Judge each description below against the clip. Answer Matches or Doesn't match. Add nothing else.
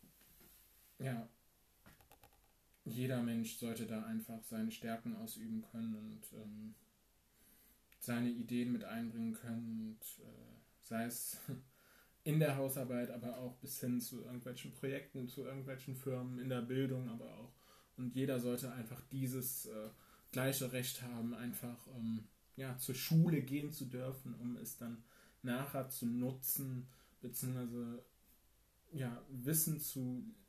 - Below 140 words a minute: Matches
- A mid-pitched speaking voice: Doesn't match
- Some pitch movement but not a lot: Doesn't match